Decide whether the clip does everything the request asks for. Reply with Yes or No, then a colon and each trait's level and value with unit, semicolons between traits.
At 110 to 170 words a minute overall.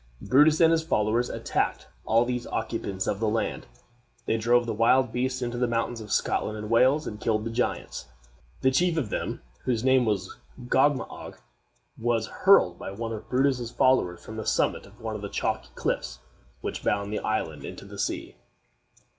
No: average, 180 wpm